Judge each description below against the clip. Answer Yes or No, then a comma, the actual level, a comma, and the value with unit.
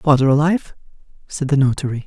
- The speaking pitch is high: No, medium, 140 Hz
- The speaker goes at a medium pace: Yes, average, 145 wpm